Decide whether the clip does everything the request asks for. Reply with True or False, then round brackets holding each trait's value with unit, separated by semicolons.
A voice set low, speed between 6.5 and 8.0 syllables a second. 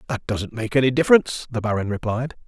True (120 Hz; 6.6 syllables/s)